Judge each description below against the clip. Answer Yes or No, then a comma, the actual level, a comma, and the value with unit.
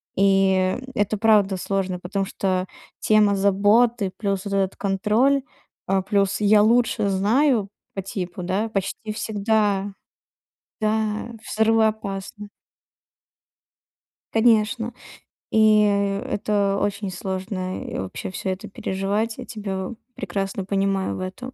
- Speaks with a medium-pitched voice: No, high, 200 Hz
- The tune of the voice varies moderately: No, narrow, 2.0 semitones